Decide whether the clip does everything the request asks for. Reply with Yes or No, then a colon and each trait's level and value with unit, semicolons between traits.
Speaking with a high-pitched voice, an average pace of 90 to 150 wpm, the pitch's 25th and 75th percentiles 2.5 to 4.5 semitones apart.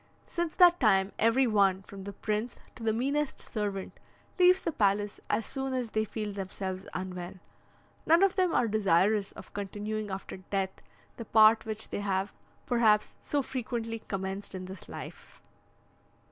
No: high, 215 Hz; average, 160 wpm; average, 3.6 semitones